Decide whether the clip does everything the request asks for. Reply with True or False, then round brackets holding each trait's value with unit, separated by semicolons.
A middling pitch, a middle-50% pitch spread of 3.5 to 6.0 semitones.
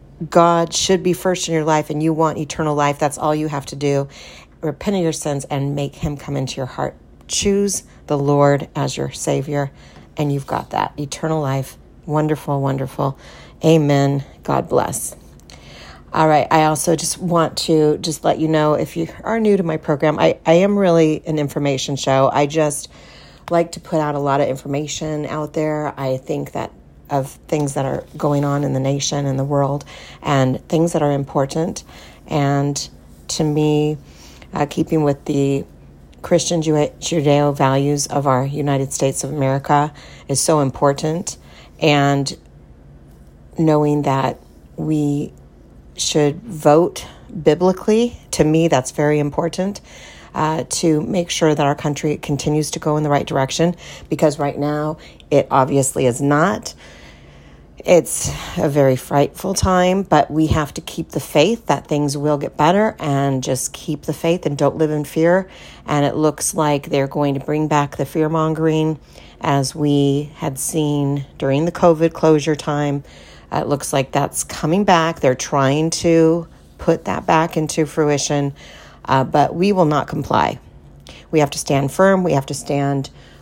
False (150 Hz; 2.4 semitones)